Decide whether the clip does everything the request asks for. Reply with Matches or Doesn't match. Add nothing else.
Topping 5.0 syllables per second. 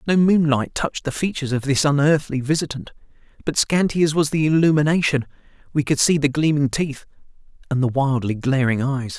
Matches